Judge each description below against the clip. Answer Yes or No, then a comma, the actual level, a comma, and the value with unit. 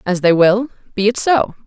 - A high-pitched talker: Yes, high, 210 Hz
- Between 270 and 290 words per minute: No, fast, 215 wpm